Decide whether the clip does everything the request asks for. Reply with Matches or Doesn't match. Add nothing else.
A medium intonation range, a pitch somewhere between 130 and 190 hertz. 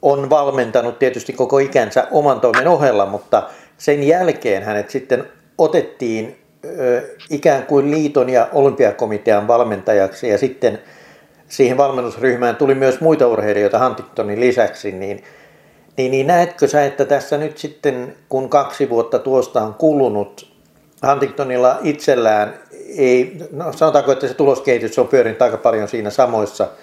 Matches